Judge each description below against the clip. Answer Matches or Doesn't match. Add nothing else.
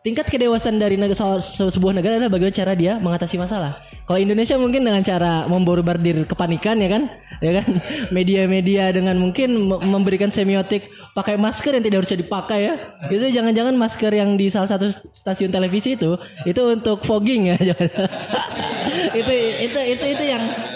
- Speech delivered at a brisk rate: Matches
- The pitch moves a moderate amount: Matches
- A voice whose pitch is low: Doesn't match